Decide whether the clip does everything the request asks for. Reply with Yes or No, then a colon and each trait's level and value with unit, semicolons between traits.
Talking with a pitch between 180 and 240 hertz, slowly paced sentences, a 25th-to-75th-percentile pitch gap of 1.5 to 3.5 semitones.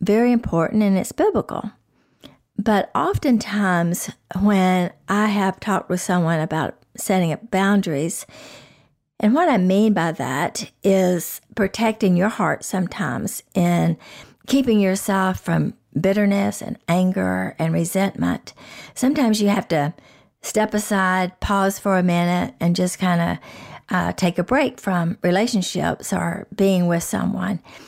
Yes: high, 190 Hz; slow, 130 wpm; average, 2.9 semitones